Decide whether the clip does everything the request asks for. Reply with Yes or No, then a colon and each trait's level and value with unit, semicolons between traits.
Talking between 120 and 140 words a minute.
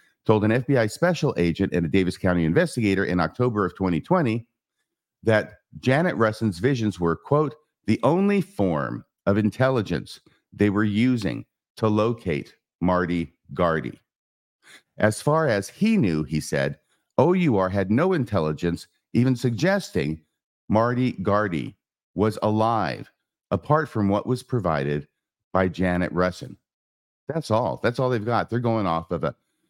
Yes: slow, 135 wpm